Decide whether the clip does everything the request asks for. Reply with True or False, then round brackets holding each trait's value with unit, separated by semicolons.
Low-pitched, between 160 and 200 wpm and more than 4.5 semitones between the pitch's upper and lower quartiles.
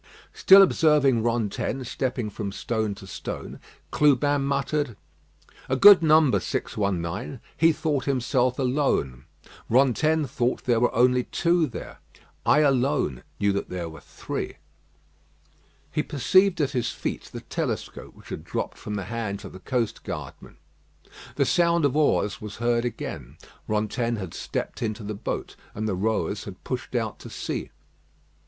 False (125 Hz; 145 wpm; 5.3 semitones)